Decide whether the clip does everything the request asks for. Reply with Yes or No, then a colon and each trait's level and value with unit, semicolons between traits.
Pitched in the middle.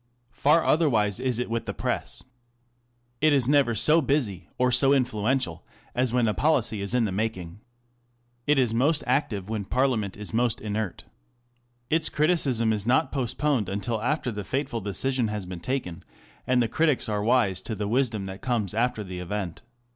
No: low, 115 Hz